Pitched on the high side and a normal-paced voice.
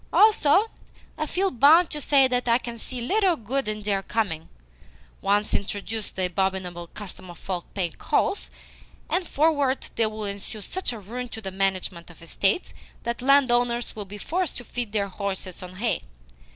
Yes: high, 220 Hz; average, 170 wpm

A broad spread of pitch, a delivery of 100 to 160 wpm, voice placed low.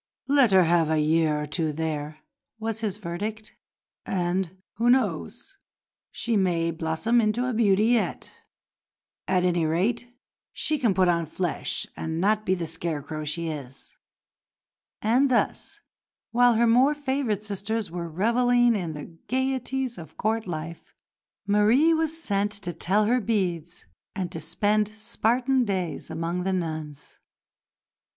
No: wide, 5.8 semitones; average, 140 wpm; high, 195 Hz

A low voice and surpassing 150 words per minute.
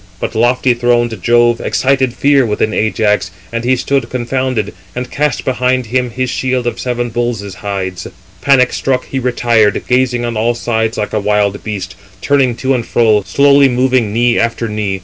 Yes: low, 120 Hz; average, 170 wpm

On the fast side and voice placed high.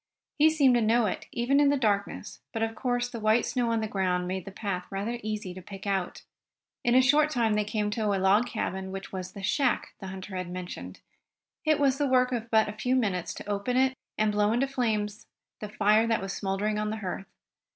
Yes: fast, 230 wpm; high, 215 Hz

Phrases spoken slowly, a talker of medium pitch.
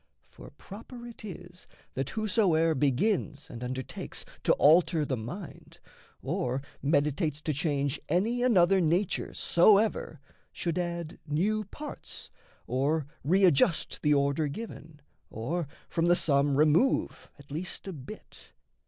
Yes: slow, 125 wpm; medium, 160 Hz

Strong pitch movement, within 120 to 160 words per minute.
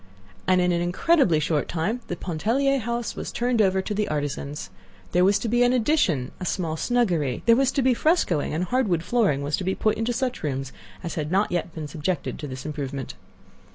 No: wide, 7.6 semitones; fast, 205 wpm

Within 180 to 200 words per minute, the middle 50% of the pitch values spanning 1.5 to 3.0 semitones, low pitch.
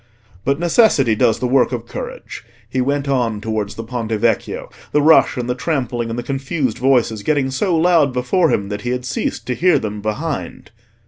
No: average, 195 wpm; average, 3.8 semitones; low, 125 Hz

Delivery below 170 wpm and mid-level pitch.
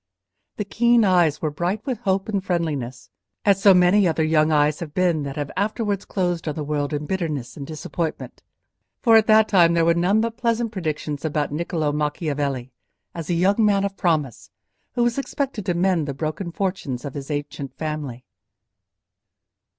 No: average, 180 wpm; medium, 170 Hz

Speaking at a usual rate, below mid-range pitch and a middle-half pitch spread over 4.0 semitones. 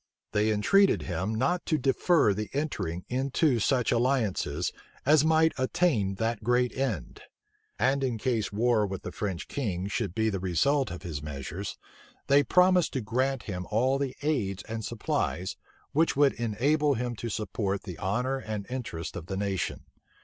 Yes: average, 165 wpm; low, 115 Hz; wide, 5.6 semitones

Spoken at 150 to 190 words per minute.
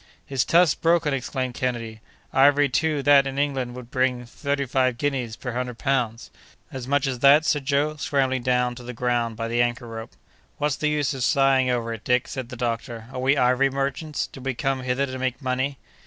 No: average, 200 wpm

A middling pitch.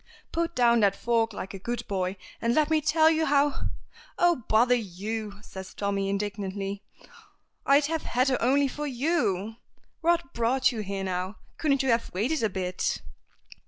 No: high, 235 Hz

